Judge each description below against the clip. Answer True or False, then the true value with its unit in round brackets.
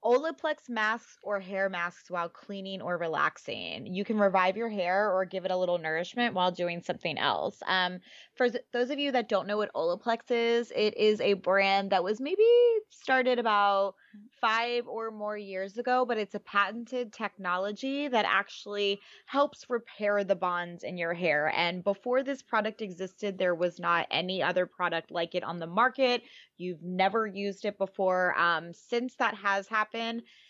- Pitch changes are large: False (4.4 semitones)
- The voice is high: True (205 Hz)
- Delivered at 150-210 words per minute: True (175 wpm)